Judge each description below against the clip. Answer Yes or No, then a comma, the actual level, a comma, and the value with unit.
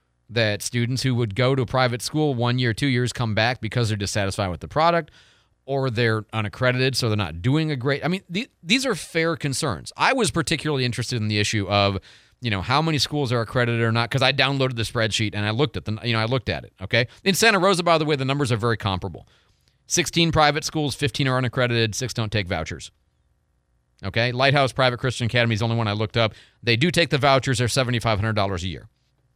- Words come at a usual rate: No, fast, 235 wpm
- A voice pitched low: Yes, low, 120 Hz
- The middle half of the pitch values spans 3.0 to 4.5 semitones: Yes, average, 4.2 semitones